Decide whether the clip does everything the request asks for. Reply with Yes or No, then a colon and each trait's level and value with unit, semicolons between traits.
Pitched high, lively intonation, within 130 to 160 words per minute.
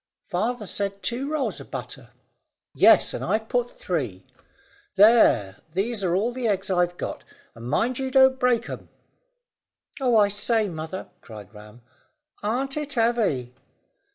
Yes: high, 210 Hz; wide, 5.7 semitones; average, 150 wpm